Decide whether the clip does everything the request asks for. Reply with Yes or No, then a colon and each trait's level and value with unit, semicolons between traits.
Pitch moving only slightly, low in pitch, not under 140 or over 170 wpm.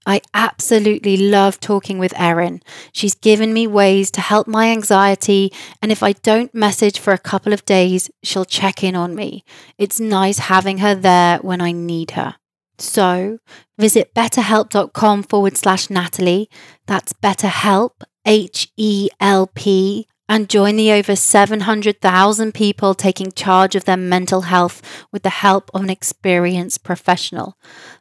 No: narrow, 2.1 semitones; high, 195 Hz; average, 150 wpm